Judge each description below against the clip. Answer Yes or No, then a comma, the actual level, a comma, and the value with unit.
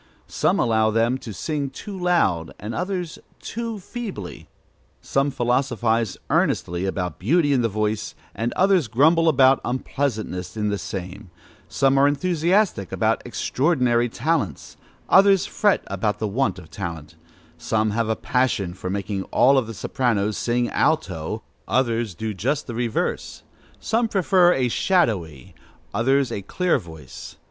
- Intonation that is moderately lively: No, wide, 6.7 semitones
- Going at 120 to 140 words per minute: Yes, slow, 135 wpm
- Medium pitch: No, low, 120 Hz